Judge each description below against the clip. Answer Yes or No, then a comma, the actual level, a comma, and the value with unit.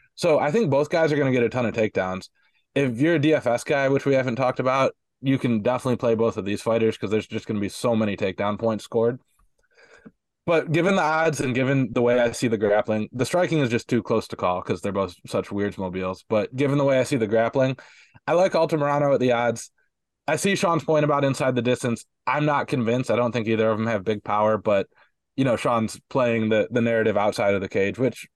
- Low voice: Yes, low, 120 Hz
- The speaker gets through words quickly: Yes, fast, 245 wpm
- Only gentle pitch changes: No, average, 4.2 semitones